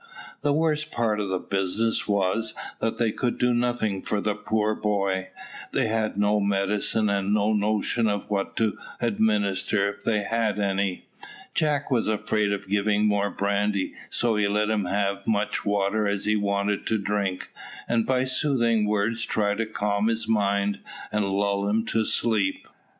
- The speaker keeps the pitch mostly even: Yes, narrow, 1.7 semitones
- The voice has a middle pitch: No, low, 105 Hz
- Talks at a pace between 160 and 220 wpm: Yes, average, 175 wpm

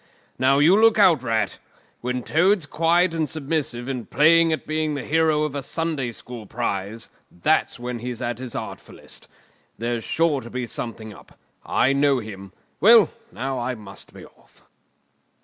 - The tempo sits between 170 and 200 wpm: No, average, 160 wpm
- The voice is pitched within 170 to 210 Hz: No, low, 135 Hz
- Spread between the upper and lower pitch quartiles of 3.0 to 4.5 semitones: No, average, 5.0 semitones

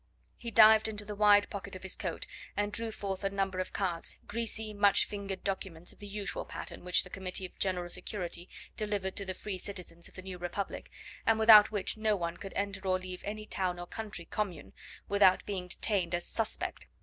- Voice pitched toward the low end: No, high, 195 Hz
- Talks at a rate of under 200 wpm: No, fast, 205 wpm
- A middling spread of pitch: No, narrow, 2.2 semitones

